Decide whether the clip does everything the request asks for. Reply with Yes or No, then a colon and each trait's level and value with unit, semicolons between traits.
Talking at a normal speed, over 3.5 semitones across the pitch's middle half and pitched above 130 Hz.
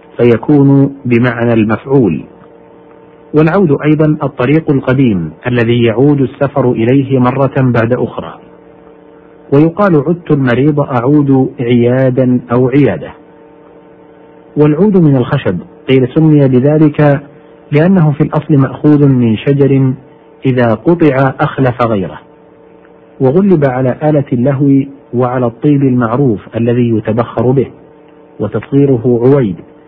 No: average, 100 wpm; average, 3.2 semitones; medium, 140 Hz